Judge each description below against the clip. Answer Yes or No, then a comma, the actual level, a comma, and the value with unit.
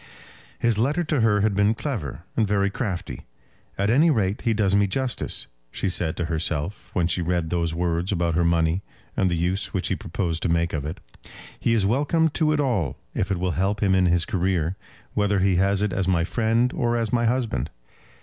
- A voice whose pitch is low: Yes, very low, 95 Hz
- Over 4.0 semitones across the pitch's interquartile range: Yes, average, 4.7 semitones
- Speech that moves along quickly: Yes, fast, 210 wpm